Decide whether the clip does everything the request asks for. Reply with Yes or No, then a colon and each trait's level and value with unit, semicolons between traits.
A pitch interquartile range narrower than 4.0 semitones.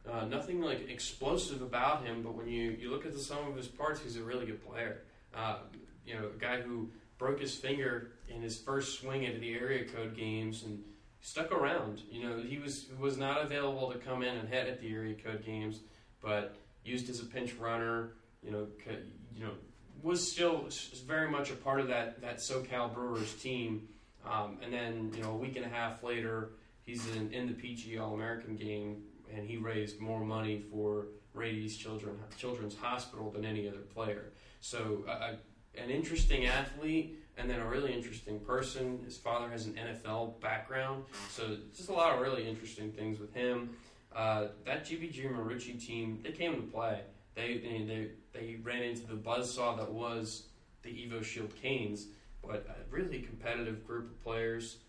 Yes: narrow, 2.4 semitones